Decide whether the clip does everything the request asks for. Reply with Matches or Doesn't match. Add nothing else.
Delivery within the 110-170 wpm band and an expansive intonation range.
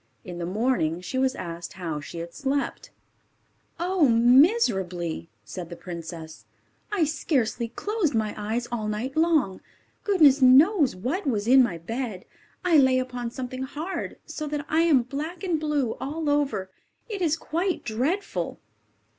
Matches